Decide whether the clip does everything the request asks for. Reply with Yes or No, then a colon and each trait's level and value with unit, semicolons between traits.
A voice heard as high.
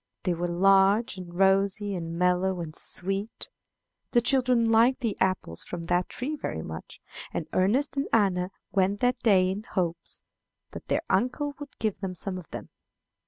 Yes: high, 195 Hz